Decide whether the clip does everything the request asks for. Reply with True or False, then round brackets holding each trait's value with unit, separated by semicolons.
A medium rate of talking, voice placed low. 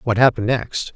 True (190 wpm; 115 Hz)